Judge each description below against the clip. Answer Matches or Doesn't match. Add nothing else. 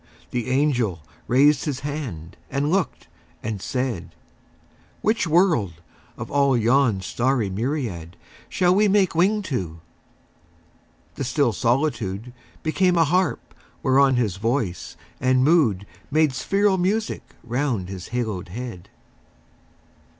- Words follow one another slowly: Matches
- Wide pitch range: Matches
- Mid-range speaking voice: Doesn't match